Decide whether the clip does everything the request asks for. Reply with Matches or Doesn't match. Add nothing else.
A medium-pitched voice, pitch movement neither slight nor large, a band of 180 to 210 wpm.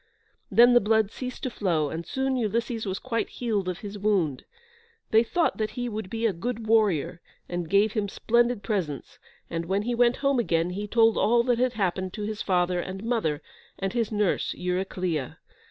Doesn't match